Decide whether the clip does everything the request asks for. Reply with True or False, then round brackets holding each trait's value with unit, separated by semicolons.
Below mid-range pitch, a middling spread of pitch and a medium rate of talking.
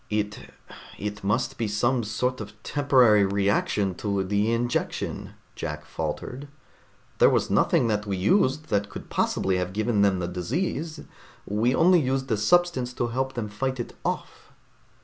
True (110 Hz; 4.4 semitones; 155 wpm)